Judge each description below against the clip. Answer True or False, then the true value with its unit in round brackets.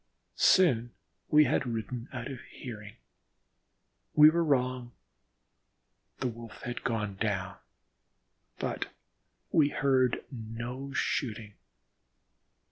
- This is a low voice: True (120 Hz)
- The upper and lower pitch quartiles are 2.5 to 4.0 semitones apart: True (3.2 semitones)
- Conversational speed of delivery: False (95 wpm)